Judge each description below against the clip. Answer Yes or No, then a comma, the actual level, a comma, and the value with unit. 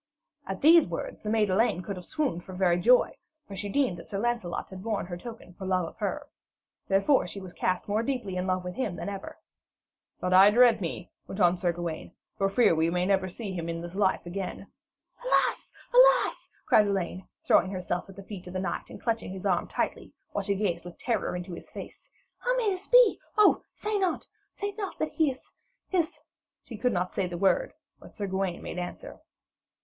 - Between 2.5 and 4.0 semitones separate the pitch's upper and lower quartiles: No, average, 4.9 semitones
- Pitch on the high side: Yes, high, 195 Hz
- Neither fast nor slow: No, fast, 215 wpm